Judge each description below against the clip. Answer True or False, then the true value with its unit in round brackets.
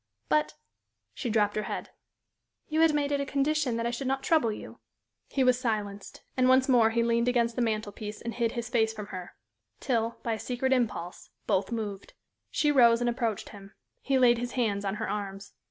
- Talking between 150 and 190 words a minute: False (205 wpm)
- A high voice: True (235 Hz)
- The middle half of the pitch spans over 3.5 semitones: False (3.2 semitones)